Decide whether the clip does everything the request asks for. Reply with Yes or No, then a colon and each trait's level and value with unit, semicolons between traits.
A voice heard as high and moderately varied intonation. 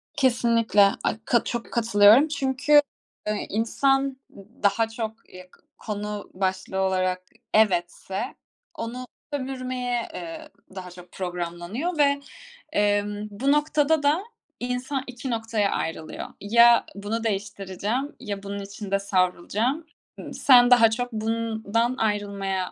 Yes: high, 225 Hz; average, 4.2 semitones